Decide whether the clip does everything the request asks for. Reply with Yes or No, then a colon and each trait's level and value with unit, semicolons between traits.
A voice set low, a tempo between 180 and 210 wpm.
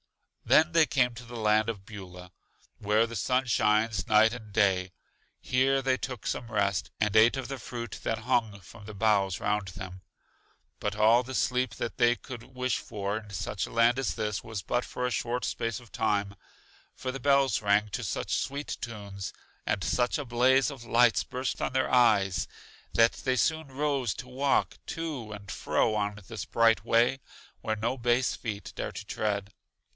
Yes: low, 115 Hz; average, 185 wpm